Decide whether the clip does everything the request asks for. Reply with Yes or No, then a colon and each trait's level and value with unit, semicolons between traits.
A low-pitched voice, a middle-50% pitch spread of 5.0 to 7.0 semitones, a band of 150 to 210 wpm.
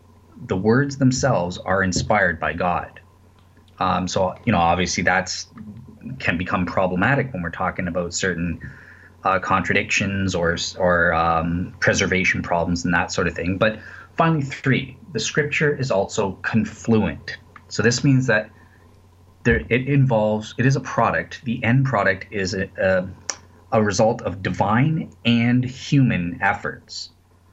No: low, 100 Hz; wide, 5.4 semitones; average, 140 wpm